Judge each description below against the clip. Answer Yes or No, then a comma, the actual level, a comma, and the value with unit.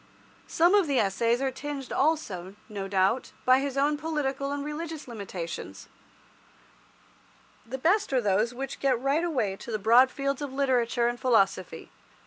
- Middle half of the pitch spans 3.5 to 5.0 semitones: Yes, average, 4.4 semitones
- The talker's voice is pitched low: No, very high, 260 Hz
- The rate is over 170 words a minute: No, average, 155 wpm